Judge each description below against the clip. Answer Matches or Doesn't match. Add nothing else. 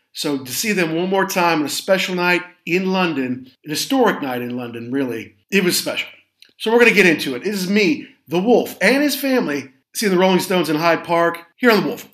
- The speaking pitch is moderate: Matches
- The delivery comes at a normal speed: Doesn't match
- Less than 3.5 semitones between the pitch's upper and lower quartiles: Doesn't match